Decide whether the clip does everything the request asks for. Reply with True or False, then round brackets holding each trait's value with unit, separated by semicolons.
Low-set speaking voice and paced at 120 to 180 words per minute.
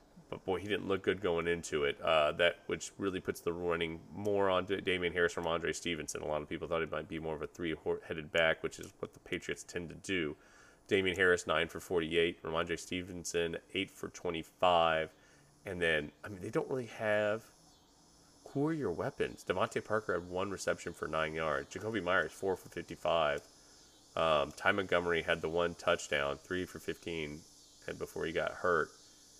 False (85 Hz; 195 wpm)